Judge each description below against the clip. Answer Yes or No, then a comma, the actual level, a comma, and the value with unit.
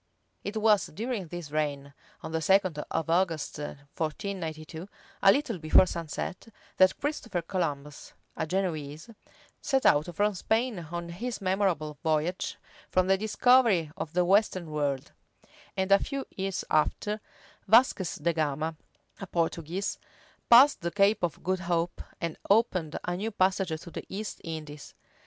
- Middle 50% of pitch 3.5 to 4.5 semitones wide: Yes, average, 4.1 semitones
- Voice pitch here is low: No, medium, 175 Hz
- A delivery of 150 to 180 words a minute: No, average, 140 wpm